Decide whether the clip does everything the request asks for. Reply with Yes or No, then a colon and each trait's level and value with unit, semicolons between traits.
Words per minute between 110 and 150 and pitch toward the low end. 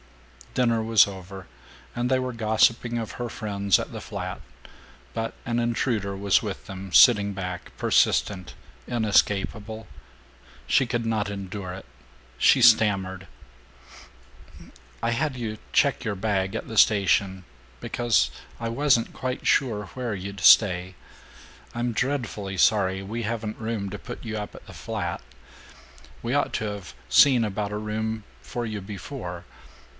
Yes: average, 140 wpm; low, 110 Hz